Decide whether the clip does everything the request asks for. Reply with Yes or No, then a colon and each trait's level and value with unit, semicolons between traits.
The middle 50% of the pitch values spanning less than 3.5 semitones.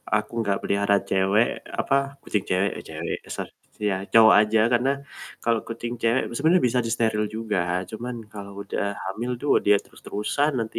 Yes: average, 2.7 semitones